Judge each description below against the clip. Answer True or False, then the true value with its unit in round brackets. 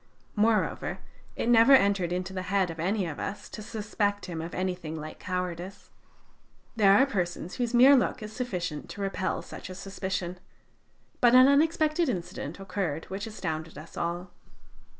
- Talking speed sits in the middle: True (160 wpm)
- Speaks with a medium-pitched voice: False (195 Hz)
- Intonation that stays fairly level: False (4.2 semitones)